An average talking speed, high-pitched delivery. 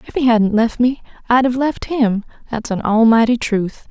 Yes: average, 185 wpm; high, 235 Hz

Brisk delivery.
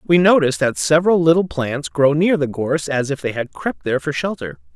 Yes: fast, 225 wpm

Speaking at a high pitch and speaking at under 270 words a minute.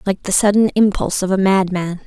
Yes: high, 195 Hz; fast, 205 wpm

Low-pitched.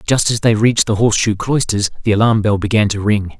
Yes: low, 110 Hz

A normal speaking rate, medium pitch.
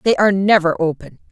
Yes: average, 185 wpm; medium, 180 Hz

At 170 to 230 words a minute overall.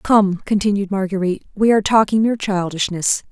No: average, 145 wpm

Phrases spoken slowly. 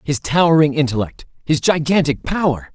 Yes: slow, 130 wpm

